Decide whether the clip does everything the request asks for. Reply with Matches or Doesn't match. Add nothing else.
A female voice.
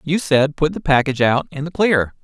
Doesn't match